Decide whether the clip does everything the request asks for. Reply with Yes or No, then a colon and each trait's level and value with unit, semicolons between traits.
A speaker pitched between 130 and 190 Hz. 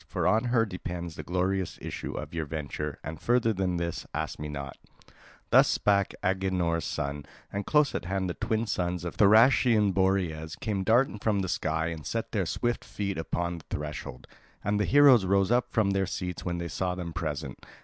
No: very low, 95 Hz